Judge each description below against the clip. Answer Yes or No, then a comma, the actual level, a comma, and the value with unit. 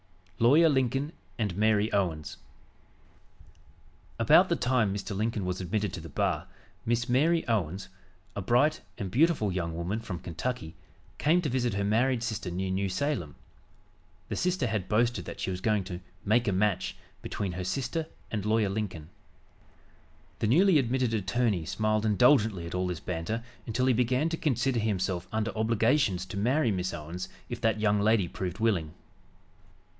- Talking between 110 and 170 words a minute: Yes, average, 160 wpm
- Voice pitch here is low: Yes, low, 110 Hz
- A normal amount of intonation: Yes, average, 4.7 semitones